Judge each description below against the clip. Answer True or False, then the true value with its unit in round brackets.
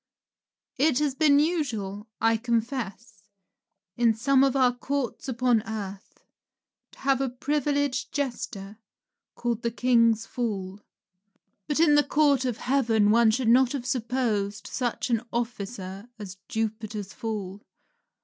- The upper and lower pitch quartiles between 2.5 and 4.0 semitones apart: True (3.5 semitones)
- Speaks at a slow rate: True (130 wpm)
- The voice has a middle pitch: False (235 Hz)